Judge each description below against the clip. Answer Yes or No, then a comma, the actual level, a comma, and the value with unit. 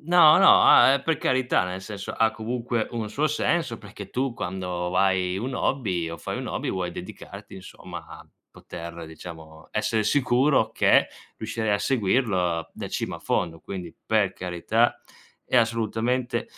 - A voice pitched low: Yes, low, 110 Hz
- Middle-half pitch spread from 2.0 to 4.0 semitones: No, wide, 5.5 semitones